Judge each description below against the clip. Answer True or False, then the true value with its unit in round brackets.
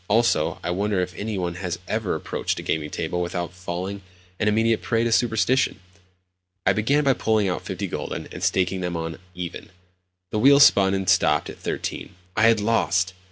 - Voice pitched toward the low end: True (95 Hz)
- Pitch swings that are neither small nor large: True (4.1 semitones)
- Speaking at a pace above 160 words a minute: True (185 wpm)